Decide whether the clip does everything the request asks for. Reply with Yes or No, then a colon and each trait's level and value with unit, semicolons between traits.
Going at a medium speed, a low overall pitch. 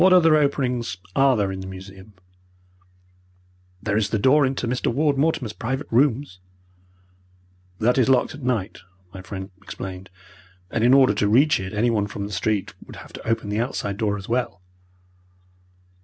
Yes: average, 170 wpm; low, 115 Hz